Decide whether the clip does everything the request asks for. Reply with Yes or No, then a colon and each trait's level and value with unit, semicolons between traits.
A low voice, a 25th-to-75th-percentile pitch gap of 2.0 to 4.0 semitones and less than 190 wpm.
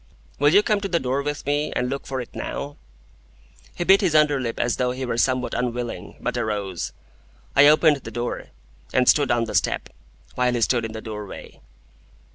No: low, 125 Hz; average, 3.5 semitones; average, 200 wpm